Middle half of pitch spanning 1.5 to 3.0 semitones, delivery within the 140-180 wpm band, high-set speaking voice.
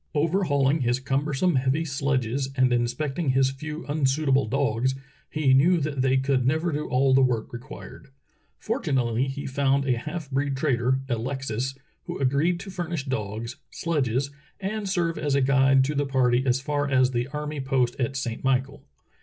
No: narrow, 2.4 semitones; average, 170 wpm; low, 135 Hz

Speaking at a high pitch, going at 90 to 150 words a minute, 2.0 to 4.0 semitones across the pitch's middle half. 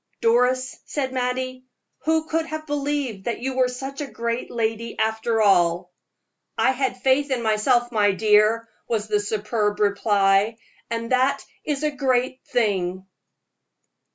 Yes: high, 235 Hz; average, 140 wpm; average, 3.6 semitones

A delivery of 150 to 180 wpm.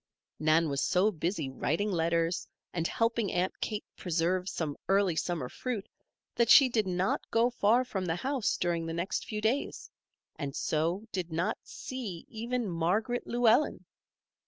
Yes: average, 155 wpm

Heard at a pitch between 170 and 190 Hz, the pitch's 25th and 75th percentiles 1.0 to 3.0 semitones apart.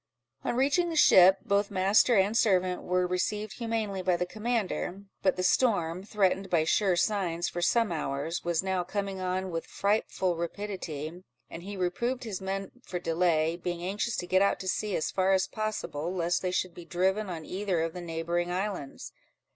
Yes: medium, 185 Hz; average, 2.7 semitones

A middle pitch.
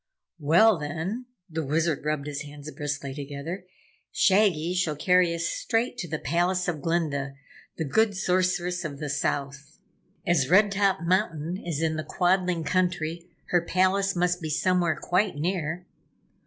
Yes: medium, 170 Hz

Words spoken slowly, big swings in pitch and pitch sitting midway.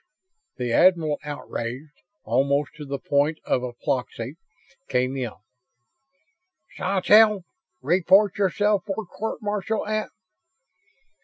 Yes: slow, 95 wpm; wide, 7.0 semitones; medium, 155 Hz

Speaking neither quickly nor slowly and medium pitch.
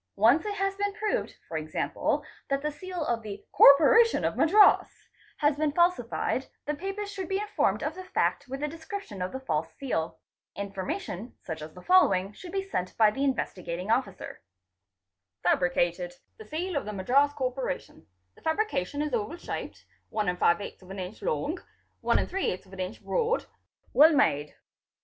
No: average, 155 wpm; very high, 275 Hz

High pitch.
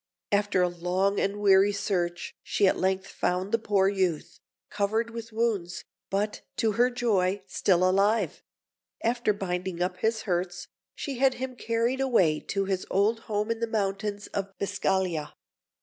Yes: high, 200 Hz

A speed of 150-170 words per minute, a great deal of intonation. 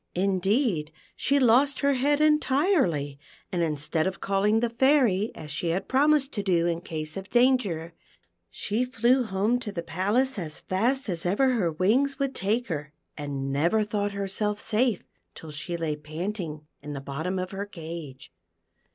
Yes: average, 165 wpm; wide, 7.0 semitones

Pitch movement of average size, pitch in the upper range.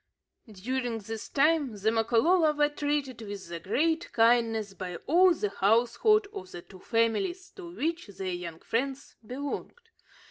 No: wide, 6.5 semitones; high, 240 Hz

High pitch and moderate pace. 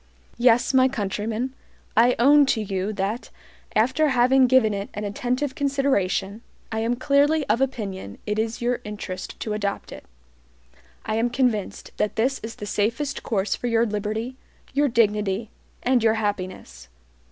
Yes: high, 225 Hz; average, 150 wpm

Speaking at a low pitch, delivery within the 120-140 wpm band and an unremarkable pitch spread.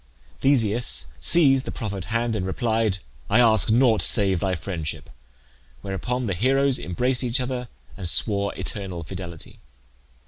Yes: low, 110 Hz; slow, 135 wpm; average, 4.7 semitones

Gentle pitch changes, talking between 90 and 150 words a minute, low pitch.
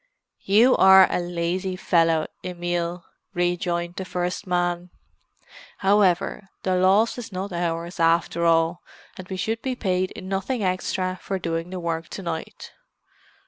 No: narrow, 1.8 semitones; average, 140 wpm; medium, 180 Hz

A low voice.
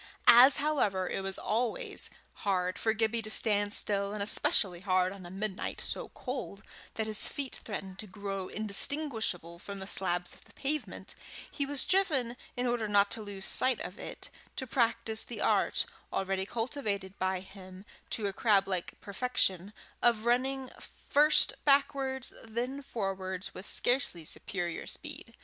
No: high, 215 Hz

